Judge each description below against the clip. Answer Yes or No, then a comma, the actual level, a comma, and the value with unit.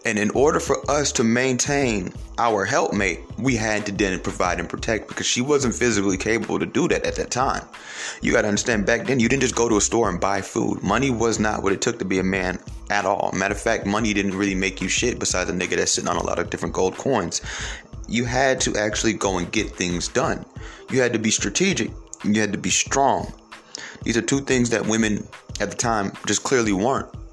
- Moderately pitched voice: No, low, 110 Hz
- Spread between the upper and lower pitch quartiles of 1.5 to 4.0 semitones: Yes, average, 3.4 semitones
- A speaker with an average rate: No, fast, 235 wpm